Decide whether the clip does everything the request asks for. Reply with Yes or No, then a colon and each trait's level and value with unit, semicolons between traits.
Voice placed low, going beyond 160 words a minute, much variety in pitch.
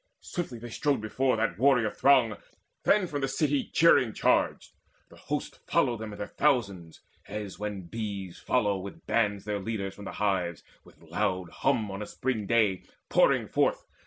No: low, 105 Hz; average, 170 wpm; average, 4.3 semitones